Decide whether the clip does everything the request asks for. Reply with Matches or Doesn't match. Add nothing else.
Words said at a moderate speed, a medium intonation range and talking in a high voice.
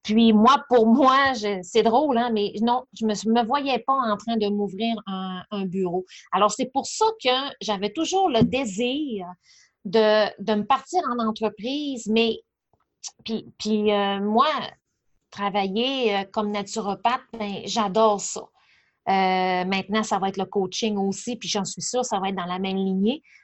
Matches